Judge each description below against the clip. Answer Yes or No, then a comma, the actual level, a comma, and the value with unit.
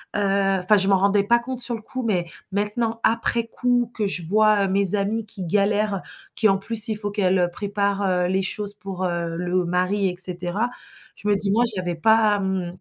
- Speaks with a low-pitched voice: No, high, 200 Hz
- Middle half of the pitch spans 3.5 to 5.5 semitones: No, narrow, 2.5 semitones